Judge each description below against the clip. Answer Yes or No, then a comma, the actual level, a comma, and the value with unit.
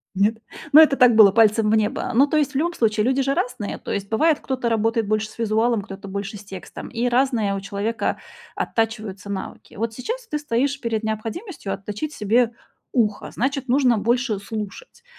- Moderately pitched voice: No, high, 225 Hz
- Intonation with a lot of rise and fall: No, average, 4.0 semitones